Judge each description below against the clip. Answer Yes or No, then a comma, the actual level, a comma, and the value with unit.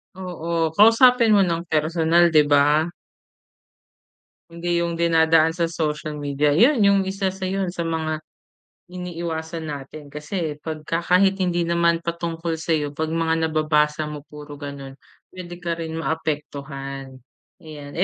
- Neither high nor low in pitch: Yes, medium, 165 Hz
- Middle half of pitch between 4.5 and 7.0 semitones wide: No, narrow, 2.4 semitones